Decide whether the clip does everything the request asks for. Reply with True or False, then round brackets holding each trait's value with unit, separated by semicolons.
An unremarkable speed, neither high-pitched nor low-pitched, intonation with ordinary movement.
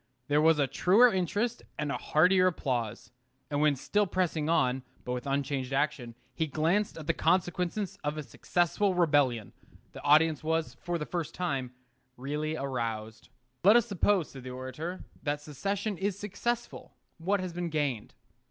True (160 wpm; 155 Hz; 5.0 semitones)